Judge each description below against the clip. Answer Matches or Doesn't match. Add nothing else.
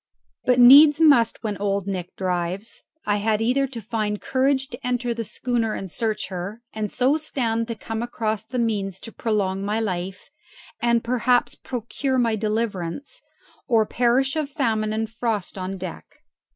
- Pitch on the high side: Matches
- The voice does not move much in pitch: Doesn't match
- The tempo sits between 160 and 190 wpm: Matches